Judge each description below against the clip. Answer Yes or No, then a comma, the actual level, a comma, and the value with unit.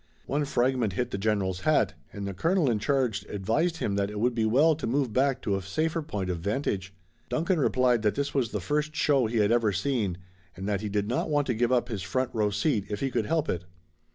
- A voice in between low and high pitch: No, low, 120 Hz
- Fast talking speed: Yes, fast, 240 wpm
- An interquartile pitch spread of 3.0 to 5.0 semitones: No, wide, 5.6 semitones